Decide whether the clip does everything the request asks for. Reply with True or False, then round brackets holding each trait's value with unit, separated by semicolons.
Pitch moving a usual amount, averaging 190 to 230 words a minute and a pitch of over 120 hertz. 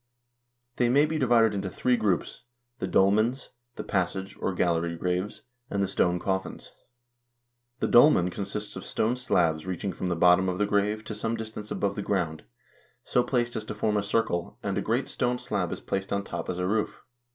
False (3.6 semitones; 195 wpm; 100 Hz)